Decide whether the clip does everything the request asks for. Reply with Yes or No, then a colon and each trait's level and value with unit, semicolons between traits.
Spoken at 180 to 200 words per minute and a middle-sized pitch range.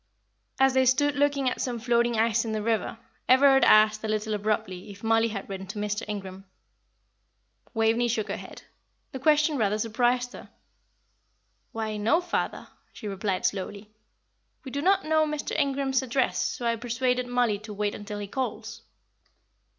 No: average, 165 wpm; average, 3.8 semitones